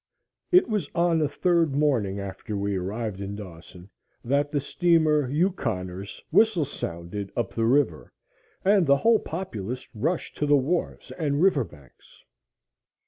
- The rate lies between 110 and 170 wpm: Yes, average, 140 wpm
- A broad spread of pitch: Yes, wide, 8.5 semitones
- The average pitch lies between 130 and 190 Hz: Yes, medium, 140 Hz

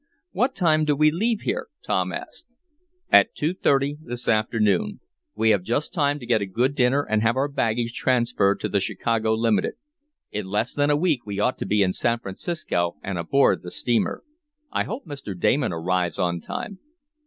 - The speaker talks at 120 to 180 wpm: No, average, 190 wpm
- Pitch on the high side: No, low, 120 Hz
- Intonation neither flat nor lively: No, wide, 6.1 semitones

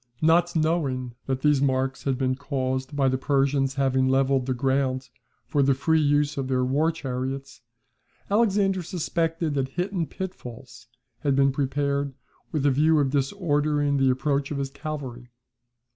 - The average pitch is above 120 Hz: Yes, medium, 140 Hz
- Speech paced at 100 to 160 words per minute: Yes, average, 155 wpm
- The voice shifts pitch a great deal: No, narrow, 2.4 semitones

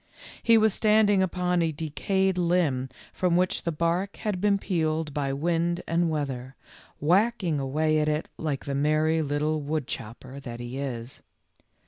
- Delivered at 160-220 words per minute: No, average, 150 wpm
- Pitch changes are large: No, average, 4.2 semitones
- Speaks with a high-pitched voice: No, medium, 160 Hz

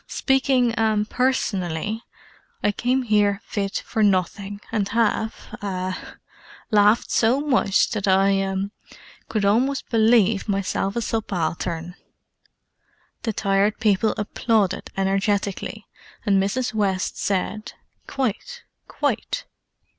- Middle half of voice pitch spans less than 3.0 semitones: Yes, narrow, 2.6 semitones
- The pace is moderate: No, slow, 85 wpm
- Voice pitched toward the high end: Yes, high, 205 Hz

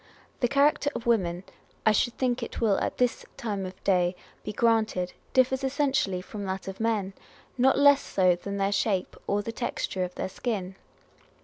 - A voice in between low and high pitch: No, high, 215 Hz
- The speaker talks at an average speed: Yes, average, 180 wpm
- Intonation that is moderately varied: Yes, average, 4.5 semitones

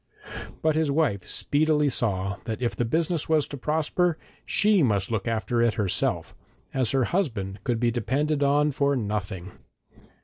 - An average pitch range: No, wide, 5.7 semitones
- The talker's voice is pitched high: No, low, 130 Hz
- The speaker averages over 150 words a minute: Yes, average, 160 wpm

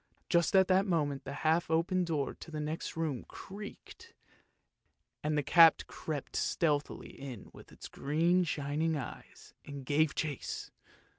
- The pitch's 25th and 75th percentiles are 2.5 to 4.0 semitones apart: Yes, average, 2.9 semitones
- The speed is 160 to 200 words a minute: No, average, 140 wpm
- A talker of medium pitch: Yes, medium, 155 Hz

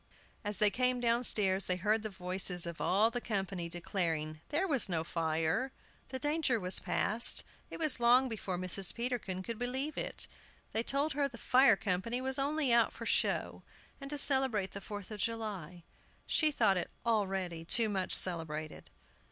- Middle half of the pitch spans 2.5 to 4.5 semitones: No, wide, 5.5 semitones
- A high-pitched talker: Yes, high, 215 Hz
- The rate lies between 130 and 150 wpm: No, average, 170 wpm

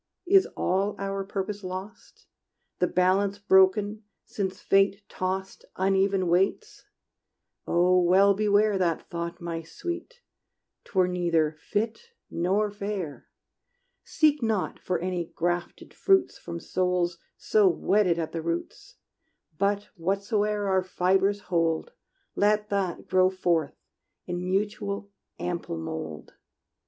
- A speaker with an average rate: No, slow, 115 wpm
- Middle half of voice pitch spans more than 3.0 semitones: No, narrow, 2.6 semitones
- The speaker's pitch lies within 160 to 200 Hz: Yes, high, 190 Hz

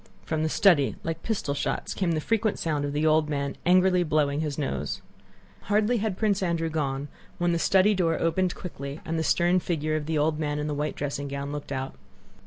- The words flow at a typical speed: No, fast, 210 wpm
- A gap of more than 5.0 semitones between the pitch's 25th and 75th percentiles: No, average, 3.6 semitones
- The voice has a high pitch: No, medium, 160 Hz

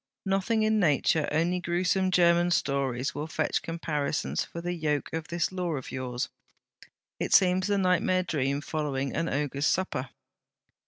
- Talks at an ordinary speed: Yes, average, 150 wpm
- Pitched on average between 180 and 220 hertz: No, medium, 165 Hz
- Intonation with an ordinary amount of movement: Yes, average, 4.4 semitones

